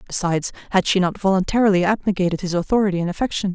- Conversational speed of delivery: Yes, average, 170 wpm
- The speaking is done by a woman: Yes, female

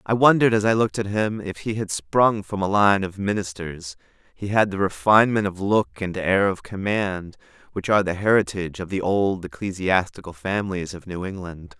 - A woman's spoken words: No, male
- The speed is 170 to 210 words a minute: Yes, average, 195 wpm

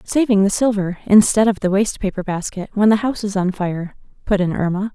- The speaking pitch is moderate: No, high, 200 Hz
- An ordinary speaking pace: No, fast, 220 wpm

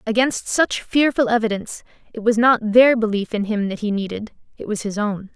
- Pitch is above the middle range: Yes, high, 220 Hz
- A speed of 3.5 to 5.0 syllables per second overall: No, 5.4 syllables/s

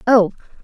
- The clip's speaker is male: No, female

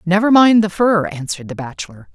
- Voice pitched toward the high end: No, medium, 180 Hz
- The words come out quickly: No, average, 195 wpm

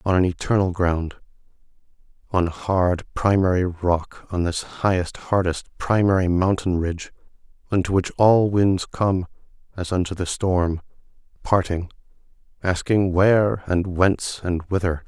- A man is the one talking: Yes, male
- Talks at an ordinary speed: No, slow, 125 wpm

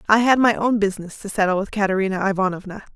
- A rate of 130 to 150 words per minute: No, fast, 205 wpm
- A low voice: No, high, 200 Hz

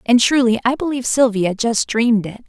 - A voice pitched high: Yes, high, 235 Hz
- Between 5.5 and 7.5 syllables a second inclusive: Yes, 5.6 syllables/s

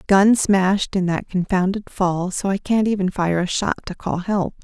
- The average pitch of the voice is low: No, high, 190 Hz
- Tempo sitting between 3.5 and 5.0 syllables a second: Yes, 4.6 syllables/s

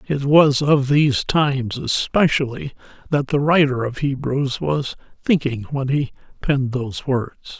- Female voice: No, male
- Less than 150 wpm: Yes, average, 140 wpm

